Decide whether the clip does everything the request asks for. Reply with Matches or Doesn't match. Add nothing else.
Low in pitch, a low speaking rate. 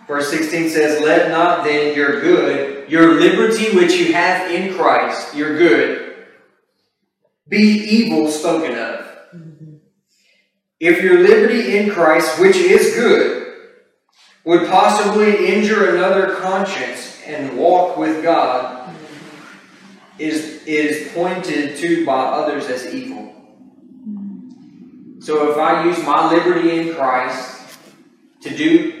Doesn't match